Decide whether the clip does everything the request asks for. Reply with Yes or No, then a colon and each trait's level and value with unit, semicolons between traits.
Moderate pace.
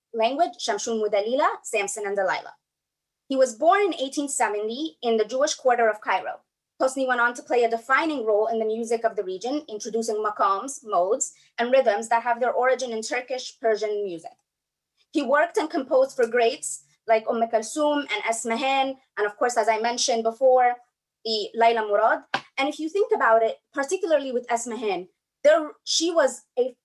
Yes: average, 175 wpm